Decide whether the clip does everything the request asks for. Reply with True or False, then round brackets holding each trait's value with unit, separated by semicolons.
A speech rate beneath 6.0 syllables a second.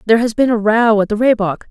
False (6.5 syllables/s)